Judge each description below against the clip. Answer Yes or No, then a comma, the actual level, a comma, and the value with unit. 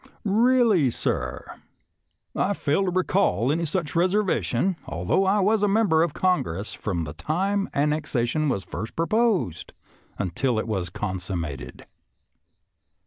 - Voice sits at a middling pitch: Yes, medium, 155 Hz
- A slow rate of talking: Yes, slow, 130 wpm